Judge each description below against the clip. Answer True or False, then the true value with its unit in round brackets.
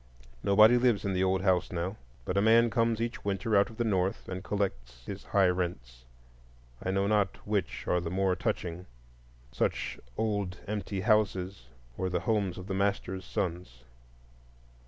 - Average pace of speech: True (160 wpm)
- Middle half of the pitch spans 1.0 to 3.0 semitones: True (2.6 semitones)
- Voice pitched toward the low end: True (95 Hz)